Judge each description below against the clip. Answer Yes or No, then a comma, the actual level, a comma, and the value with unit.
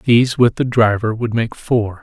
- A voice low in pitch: Yes, low, 115 Hz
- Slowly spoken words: No, fast, 205 wpm